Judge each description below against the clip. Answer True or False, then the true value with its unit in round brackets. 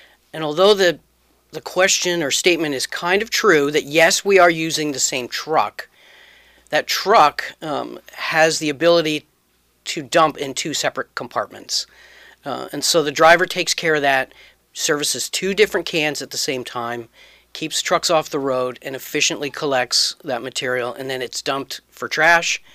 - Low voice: False (155 Hz)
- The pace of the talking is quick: False (170 wpm)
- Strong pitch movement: False (4.4 semitones)